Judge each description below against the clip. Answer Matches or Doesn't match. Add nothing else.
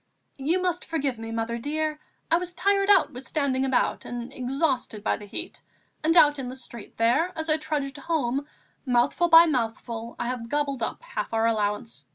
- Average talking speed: Matches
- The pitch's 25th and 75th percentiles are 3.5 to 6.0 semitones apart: Matches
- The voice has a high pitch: Matches